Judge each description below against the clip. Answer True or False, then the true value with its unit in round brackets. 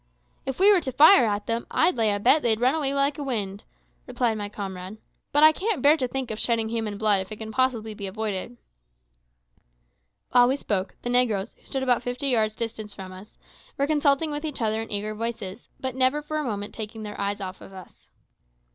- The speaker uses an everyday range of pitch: True (4.4 semitones)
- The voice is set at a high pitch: True (230 Hz)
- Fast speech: True (215 wpm)